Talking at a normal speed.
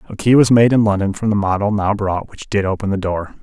No: fast, 280 wpm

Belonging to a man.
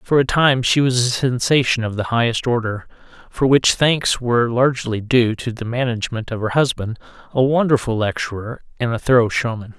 Yes: male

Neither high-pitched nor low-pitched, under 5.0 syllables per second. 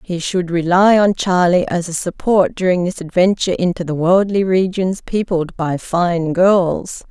Yes: medium, 180 Hz; 4.2 syllables/s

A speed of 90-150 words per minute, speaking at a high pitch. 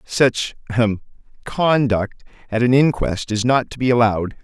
No: slow, 135 wpm; low, 120 Hz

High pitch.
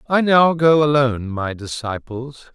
No: low, 135 Hz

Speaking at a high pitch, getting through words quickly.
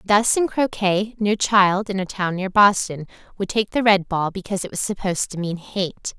Yes: high, 195 Hz; fast, 215 wpm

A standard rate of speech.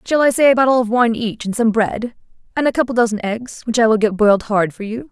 No: fast, 295 wpm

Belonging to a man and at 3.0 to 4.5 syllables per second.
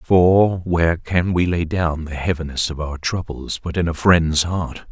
Yes: male; 4.3 syllables/s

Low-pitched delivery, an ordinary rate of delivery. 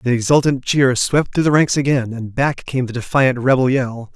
No: low, 130 Hz; fast, 215 wpm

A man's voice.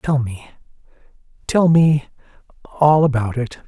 Yes: male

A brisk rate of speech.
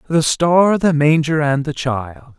No: average, 175 wpm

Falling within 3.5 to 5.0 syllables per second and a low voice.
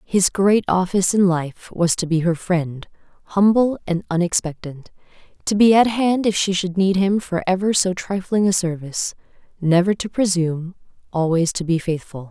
No: 4.9 syllables/s; medium, 185 Hz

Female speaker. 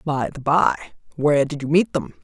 Yes: female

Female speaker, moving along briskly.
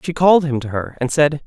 No: male; fast, 285 wpm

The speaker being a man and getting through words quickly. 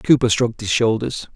No: male; average, 175 wpm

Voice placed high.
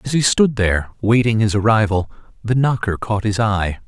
No: low, 110 Hz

